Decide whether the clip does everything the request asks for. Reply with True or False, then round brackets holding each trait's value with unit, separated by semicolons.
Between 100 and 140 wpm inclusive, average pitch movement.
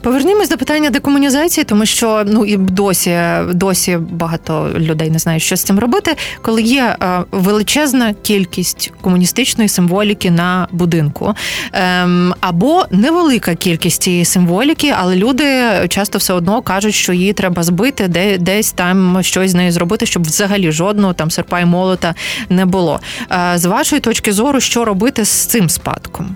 False (150 wpm; 4.3 semitones)